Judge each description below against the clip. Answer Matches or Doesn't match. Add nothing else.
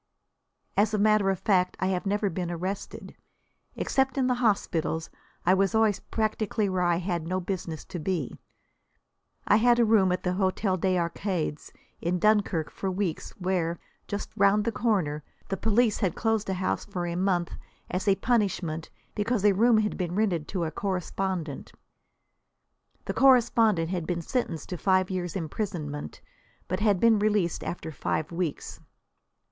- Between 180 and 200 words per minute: Doesn't match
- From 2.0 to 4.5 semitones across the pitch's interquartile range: Matches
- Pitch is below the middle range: Doesn't match